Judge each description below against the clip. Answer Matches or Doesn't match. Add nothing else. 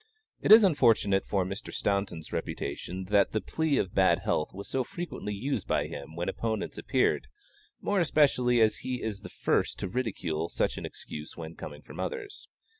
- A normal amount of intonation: Doesn't match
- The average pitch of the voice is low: Matches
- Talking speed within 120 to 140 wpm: Doesn't match